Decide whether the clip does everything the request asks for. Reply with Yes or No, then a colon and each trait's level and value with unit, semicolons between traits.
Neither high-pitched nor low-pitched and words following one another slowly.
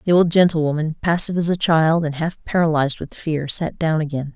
No: medium, 160 Hz; fast, 205 wpm